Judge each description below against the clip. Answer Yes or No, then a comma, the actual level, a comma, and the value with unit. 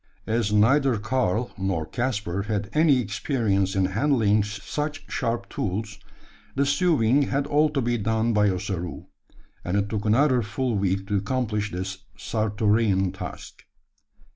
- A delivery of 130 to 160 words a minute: Yes, average, 140 wpm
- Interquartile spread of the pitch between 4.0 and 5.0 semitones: Yes, average, 4.3 semitones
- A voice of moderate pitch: No, low, 110 Hz